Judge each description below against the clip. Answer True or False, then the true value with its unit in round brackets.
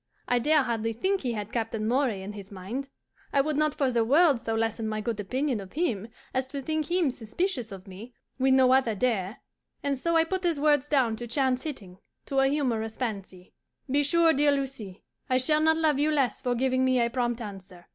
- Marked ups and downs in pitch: False (4.5 semitones)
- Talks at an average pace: False (215 wpm)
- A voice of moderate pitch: False (255 Hz)